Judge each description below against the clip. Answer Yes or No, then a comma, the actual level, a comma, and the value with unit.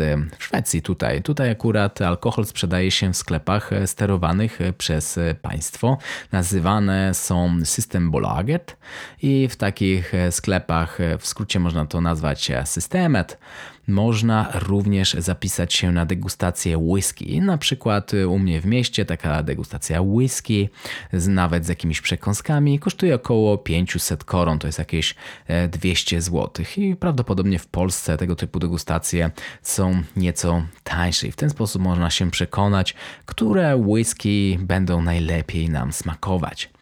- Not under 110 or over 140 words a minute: Yes, average, 130 wpm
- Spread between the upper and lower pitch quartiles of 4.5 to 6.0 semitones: No, average, 3.3 semitones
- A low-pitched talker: Yes, very low, 90 Hz